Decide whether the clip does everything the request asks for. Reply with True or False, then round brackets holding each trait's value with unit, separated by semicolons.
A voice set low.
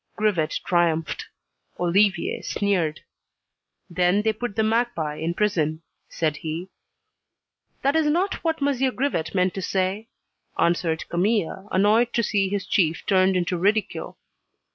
False (190 Hz)